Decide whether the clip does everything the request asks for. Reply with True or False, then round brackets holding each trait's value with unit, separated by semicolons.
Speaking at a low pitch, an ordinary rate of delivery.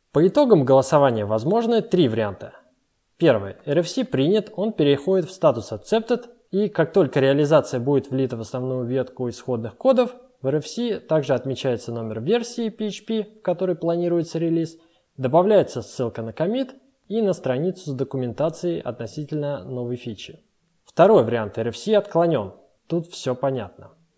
False (155 Hz; 135 wpm)